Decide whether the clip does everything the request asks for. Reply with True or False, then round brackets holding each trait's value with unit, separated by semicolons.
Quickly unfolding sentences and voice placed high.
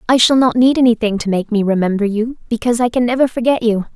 True (245 wpm; 230 Hz)